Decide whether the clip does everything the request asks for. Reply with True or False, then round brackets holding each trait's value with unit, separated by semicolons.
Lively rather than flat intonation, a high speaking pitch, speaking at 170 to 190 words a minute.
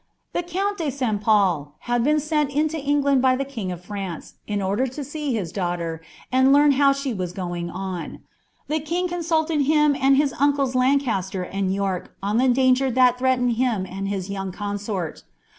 True (6.4 semitones; 255 Hz; 180 wpm)